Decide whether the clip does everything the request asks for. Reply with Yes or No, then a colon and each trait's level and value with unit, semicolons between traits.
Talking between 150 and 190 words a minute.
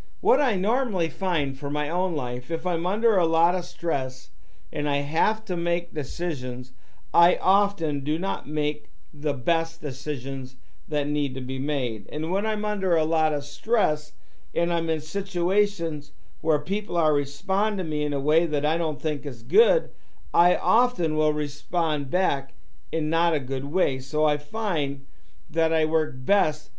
Yes: average, 175 wpm